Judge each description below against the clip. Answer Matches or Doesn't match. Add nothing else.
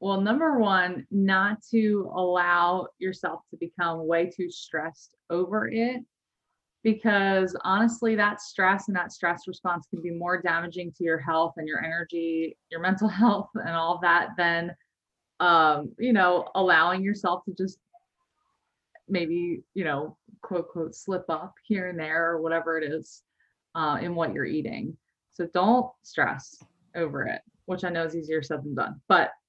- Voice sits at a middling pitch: Matches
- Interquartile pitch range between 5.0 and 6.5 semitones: Doesn't match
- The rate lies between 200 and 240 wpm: Doesn't match